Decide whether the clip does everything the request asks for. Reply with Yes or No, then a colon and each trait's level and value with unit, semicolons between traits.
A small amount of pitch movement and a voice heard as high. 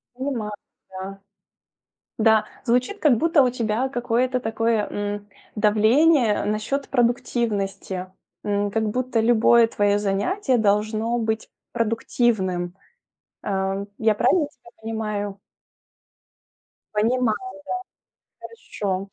No: average, 3.0 semitones; high, 220 Hz